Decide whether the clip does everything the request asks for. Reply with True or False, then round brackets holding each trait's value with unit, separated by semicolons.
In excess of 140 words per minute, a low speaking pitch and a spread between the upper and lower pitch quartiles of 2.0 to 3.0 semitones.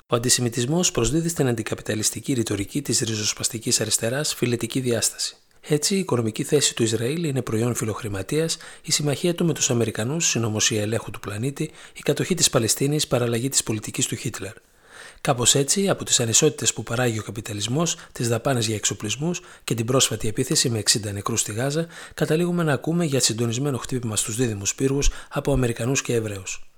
False (165 wpm; 125 Hz; 4.6 semitones)